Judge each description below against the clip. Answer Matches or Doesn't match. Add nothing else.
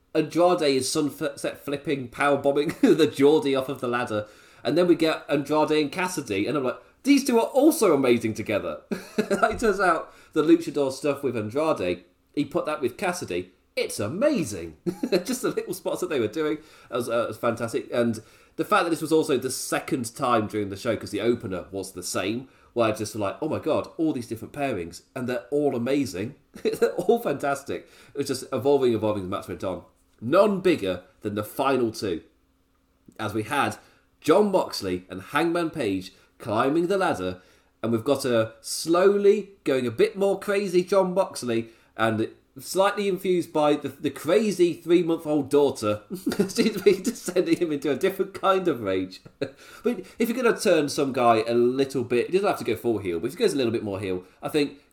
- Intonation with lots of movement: Matches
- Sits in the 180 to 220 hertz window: Doesn't match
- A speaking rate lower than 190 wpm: Doesn't match